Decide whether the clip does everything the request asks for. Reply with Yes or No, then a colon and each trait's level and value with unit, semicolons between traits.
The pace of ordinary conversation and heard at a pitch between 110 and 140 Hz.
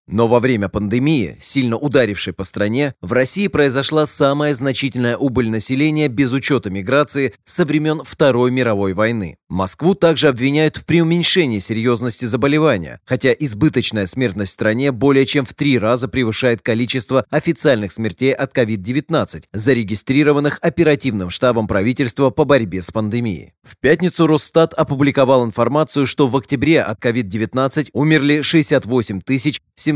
Yes: average, 135 wpm; low, 135 Hz